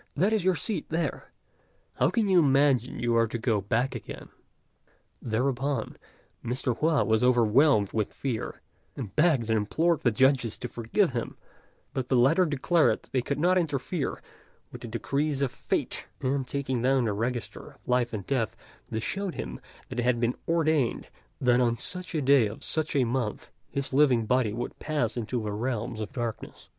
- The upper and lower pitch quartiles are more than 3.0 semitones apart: Yes, average, 4.0 semitones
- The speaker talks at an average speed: Yes, average, 180 wpm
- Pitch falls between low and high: No, low, 125 Hz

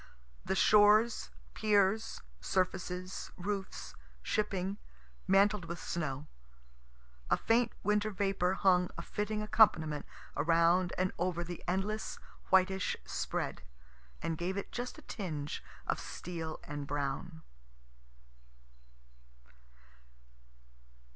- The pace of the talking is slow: Yes, slow, 95 wpm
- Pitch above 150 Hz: Yes, medium, 185 Hz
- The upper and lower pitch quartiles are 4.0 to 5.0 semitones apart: No, average, 3.6 semitones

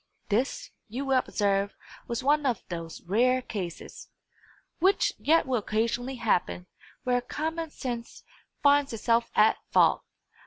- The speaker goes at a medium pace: No, slow, 125 wpm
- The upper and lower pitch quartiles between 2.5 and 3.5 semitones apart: No, average, 4.4 semitones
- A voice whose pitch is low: No, high, 245 Hz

